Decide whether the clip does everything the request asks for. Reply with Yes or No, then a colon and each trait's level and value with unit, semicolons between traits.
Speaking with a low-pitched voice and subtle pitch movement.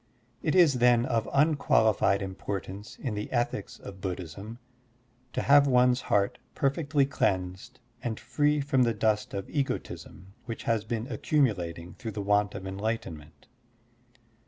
No: low, 110 Hz; average, 5.3 semitones